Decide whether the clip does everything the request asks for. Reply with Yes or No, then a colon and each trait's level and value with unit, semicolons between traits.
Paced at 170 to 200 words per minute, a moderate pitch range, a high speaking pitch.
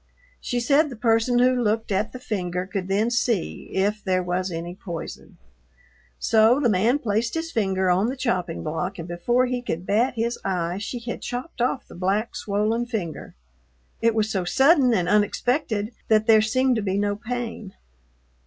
Yes: average, 180 wpm; average, 4.3 semitones; high, 215 Hz